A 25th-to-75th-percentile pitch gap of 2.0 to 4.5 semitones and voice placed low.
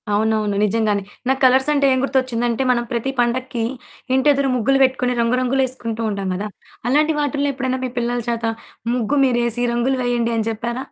No: narrow, 2.4 semitones; high, 245 Hz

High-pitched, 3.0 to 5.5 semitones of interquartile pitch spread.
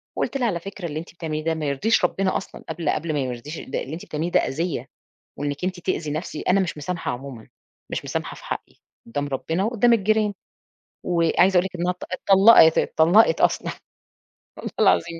No: medium, 170 Hz; average, 3.9 semitones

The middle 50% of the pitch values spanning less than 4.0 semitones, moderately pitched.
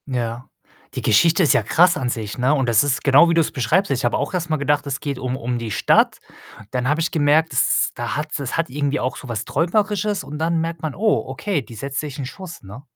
No: average, 4.6 semitones; medium, 145 Hz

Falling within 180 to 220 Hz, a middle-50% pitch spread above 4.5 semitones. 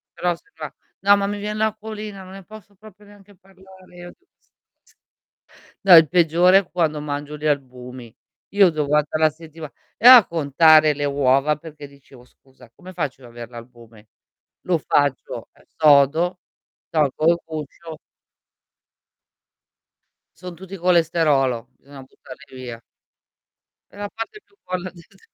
No: medium, 160 Hz; average, 5.1 semitones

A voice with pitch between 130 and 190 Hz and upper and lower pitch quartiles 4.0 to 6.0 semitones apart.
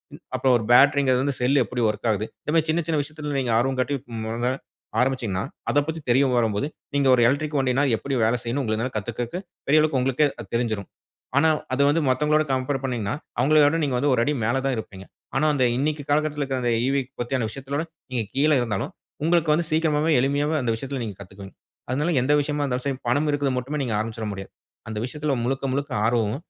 No: low, 135 Hz; average, 3.5 semitones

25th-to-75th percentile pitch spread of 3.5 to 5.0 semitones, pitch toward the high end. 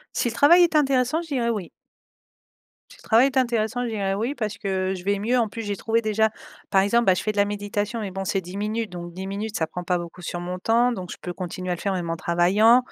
Yes: average, 4.0 semitones; high, 205 Hz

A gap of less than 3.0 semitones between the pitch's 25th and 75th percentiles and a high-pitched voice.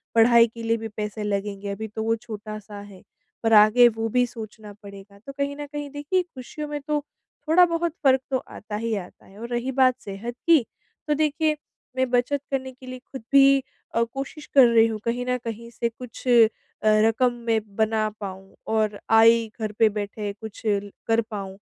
No: average, 3.5 semitones; high, 230 Hz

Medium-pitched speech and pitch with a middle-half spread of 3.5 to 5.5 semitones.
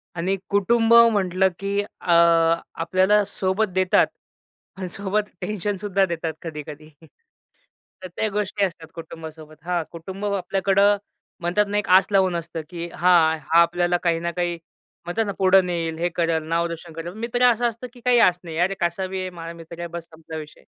No: medium, 180 Hz; average, 3.1 semitones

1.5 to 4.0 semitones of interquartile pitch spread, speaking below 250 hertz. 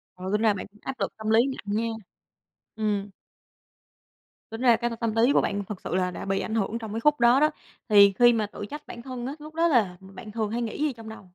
Yes: average, 2.8 semitones; high, 225 Hz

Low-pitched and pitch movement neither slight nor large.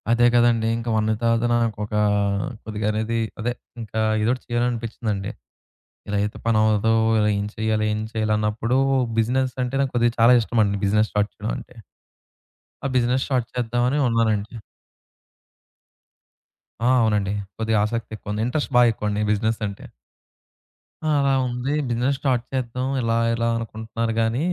No: low, 115 Hz; narrow, 2.0 semitones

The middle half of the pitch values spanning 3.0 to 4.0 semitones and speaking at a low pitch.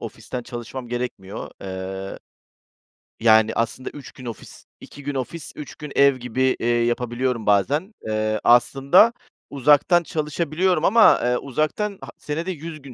No: average, 4.7 semitones; low, 130 Hz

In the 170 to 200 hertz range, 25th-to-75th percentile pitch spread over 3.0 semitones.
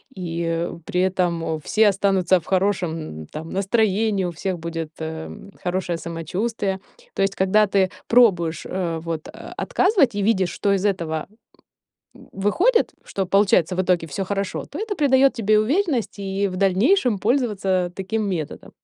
Yes: high, 190 Hz; average, 3.6 semitones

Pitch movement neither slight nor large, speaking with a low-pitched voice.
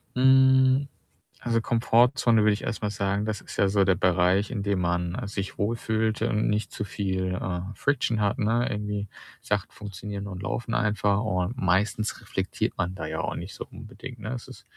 Yes: average, 3.0 semitones; low, 105 Hz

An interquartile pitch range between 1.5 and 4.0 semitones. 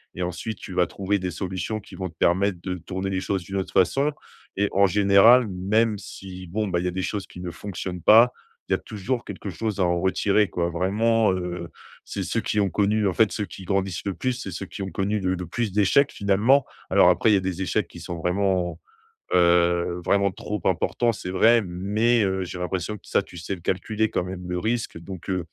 Yes: average, 2.8 semitones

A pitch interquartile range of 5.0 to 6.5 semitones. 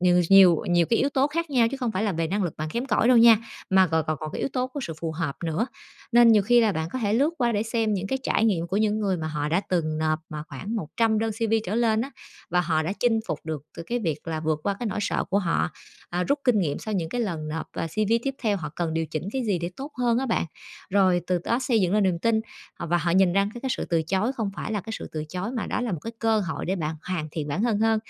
Yes: wide, 5.5 semitones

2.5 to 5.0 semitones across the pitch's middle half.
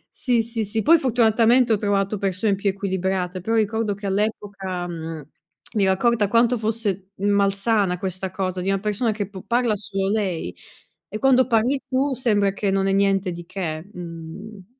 Yes: average, 2.8 semitones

